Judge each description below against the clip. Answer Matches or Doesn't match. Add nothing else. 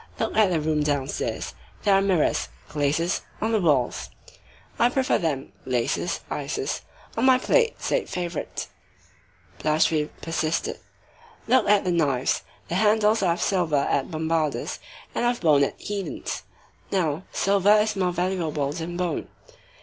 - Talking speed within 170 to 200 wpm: Doesn't match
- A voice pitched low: Doesn't match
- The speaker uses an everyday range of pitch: Matches